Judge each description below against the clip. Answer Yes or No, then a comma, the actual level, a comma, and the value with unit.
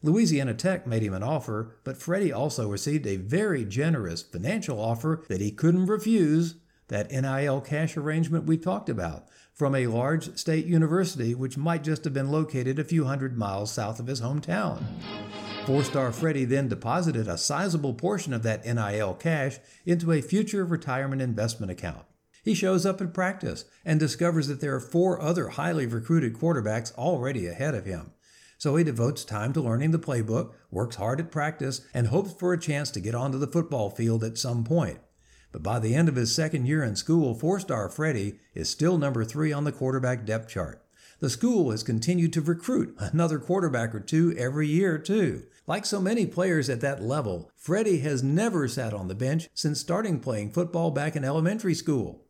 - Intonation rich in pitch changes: Yes, wide, 6.2 semitones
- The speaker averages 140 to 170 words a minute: No, average, 190 wpm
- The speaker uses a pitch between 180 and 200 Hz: No, medium, 145 Hz